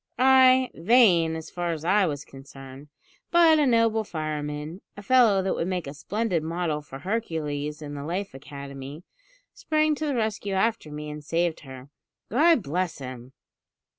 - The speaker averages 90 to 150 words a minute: No, average, 165 wpm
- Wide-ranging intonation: Yes, wide, 7.0 semitones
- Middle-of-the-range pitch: Yes, medium, 170 Hz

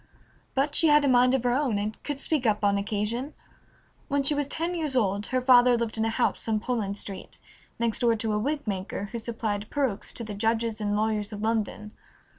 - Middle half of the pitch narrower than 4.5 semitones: Yes, average, 3.7 semitones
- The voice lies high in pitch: Yes, high, 230 Hz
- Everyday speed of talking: No, fast, 220 wpm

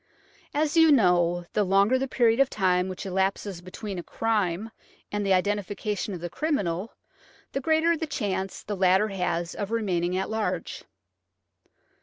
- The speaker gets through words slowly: No, average, 150 wpm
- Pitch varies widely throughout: No, average, 3.7 semitones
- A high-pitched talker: Yes, high, 200 Hz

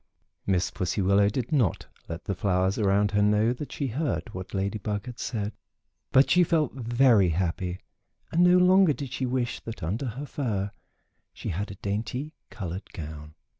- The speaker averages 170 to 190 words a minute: Yes, average, 175 wpm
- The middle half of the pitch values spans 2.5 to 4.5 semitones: No, average, 5.3 semitones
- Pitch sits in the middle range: No, low, 105 Hz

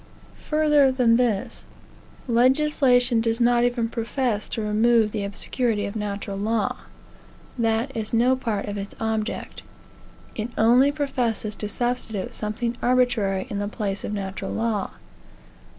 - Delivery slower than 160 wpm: Yes, slow, 135 wpm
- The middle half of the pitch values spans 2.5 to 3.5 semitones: Yes, average, 2.8 semitones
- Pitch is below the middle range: No, high, 230 Hz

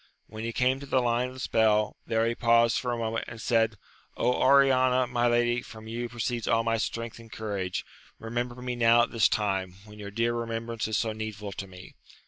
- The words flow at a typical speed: No, fast, 210 wpm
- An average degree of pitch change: No, narrow, 1.7 semitones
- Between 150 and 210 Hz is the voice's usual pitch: No, low, 115 Hz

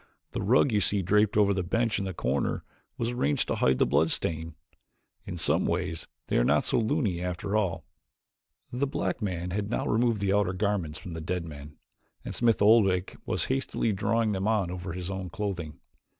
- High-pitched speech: No, very low, 95 Hz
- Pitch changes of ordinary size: Yes, average, 3.7 semitones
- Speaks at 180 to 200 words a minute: Yes, average, 195 wpm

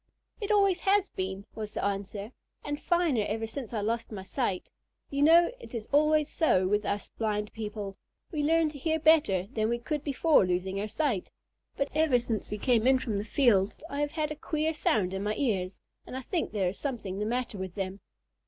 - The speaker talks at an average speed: No, fast, 215 wpm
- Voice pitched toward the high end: Yes, high, 230 Hz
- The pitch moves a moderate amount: No, wide, 6.7 semitones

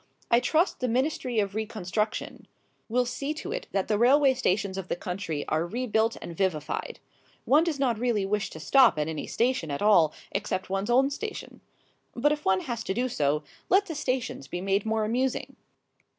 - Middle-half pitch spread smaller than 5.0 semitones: No, average, 5.3 semitones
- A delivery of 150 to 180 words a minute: No, average, 190 wpm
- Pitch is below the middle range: No, high, 220 Hz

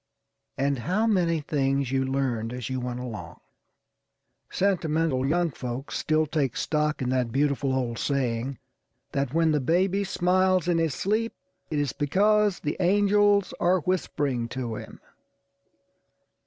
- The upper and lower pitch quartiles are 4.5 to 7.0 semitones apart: Yes, wide, 5.6 semitones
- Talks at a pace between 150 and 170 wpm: No, average, 140 wpm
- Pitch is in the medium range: Yes, medium, 150 Hz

